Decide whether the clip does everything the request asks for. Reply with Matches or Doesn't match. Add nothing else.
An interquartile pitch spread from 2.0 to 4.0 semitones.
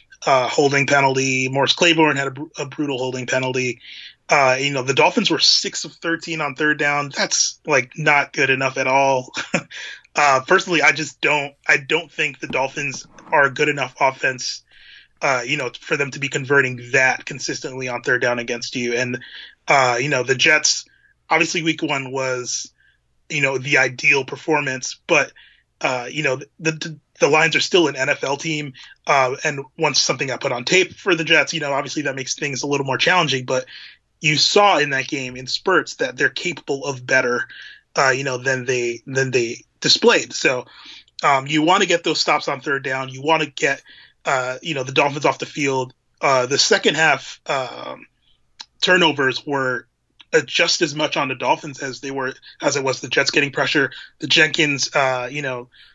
Matches